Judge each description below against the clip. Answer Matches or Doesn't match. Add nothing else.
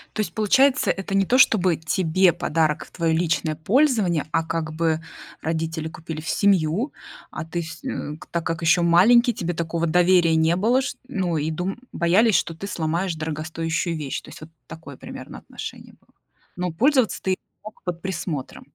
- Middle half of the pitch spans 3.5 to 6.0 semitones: Doesn't match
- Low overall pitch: Doesn't match